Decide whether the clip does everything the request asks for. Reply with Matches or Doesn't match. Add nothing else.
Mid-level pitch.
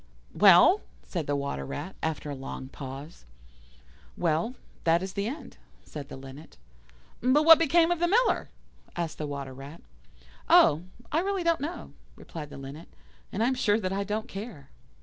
Matches